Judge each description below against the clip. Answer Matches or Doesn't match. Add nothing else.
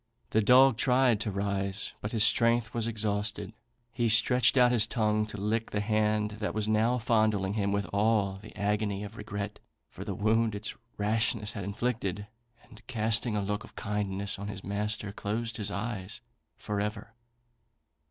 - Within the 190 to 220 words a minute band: Doesn't match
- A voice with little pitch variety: Matches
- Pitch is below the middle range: Matches